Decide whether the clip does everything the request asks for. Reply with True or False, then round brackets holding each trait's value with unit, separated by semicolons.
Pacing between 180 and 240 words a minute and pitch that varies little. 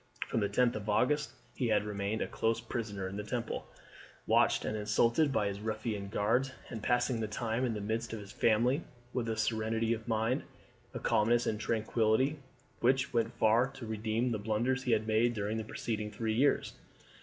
True (190 wpm; 2.0 semitones)